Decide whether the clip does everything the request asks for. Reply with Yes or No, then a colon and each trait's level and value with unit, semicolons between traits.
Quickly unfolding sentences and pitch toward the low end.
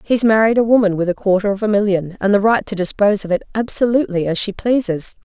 No: fast, 240 wpm; high, 205 Hz